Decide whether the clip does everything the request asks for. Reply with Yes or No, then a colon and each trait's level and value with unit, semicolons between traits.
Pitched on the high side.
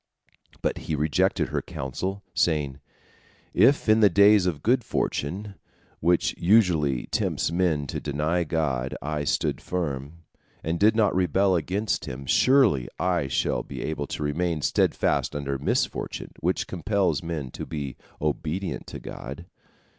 No: very low, 85 Hz